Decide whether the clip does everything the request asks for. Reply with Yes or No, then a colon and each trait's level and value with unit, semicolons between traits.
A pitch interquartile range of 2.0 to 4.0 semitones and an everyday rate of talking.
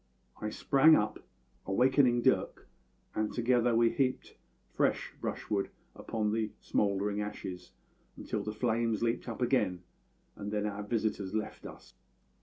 No: narrow, 2.5 semitones; slow, 130 wpm